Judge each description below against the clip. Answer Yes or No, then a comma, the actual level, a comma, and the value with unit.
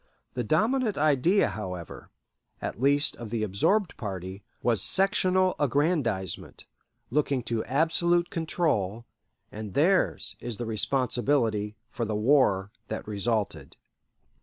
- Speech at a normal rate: No, slow, 110 wpm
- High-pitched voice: No, low, 120 Hz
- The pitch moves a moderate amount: No, wide, 7.0 semitones